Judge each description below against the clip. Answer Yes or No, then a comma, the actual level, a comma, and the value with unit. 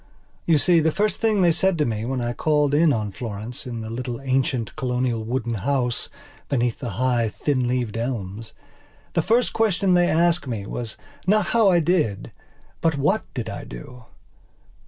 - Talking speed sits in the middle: Yes, average, 175 wpm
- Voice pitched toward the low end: Yes, low, 130 Hz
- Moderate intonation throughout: No, wide, 6.2 semitones